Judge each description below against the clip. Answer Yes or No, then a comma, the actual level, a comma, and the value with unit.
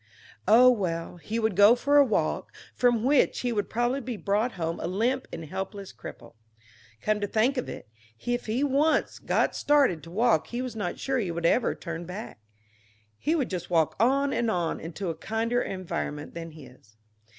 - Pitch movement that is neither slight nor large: No, wide, 6.2 semitones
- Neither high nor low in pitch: No, high, 215 Hz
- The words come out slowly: No, average, 190 wpm